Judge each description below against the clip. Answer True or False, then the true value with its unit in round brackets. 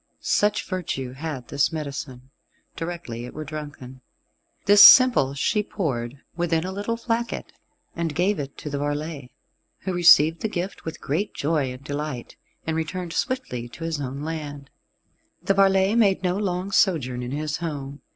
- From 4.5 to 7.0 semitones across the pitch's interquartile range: True (5.0 semitones)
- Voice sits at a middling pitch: True (160 Hz)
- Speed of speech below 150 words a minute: False (160 wpm)